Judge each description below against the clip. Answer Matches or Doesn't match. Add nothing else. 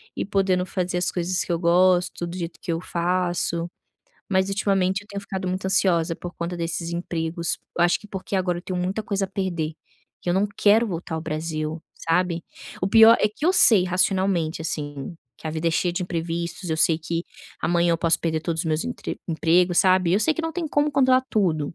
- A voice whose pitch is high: Doesn't match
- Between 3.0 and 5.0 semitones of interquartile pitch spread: Doesn't match